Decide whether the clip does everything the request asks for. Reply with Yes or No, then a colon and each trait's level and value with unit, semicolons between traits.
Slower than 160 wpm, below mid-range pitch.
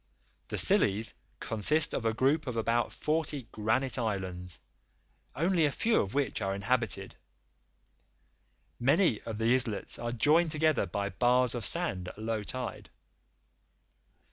Yes: slow, 135 wpm; low, 120 Hz